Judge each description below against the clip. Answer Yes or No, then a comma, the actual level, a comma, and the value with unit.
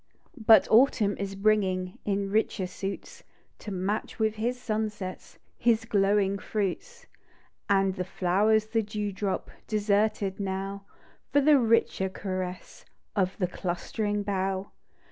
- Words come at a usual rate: No, slow, 125 wpm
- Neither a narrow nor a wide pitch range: No, narrow, 2.2 semitones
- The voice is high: Yes, high, 200 Hz